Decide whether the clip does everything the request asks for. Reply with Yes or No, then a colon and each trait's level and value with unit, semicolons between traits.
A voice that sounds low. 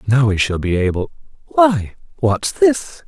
Yes: low, 110 Hz